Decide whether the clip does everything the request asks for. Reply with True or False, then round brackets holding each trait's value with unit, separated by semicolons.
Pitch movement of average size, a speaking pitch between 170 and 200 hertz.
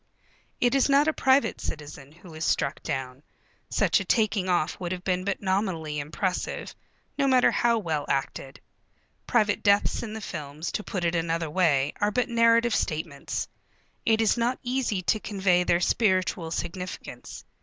False (5.8 semitones; 185 Hz)